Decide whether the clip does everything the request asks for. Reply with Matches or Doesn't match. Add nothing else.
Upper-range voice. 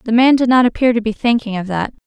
Matches